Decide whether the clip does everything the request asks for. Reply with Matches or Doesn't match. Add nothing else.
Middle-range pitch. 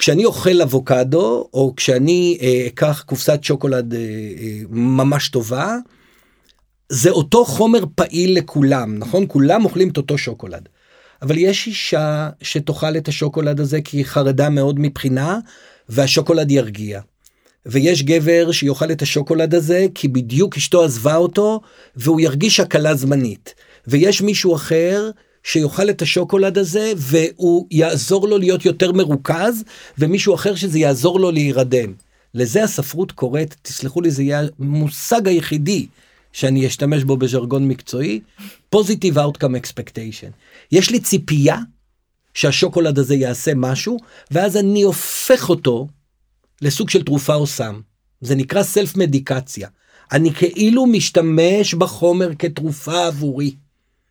Matches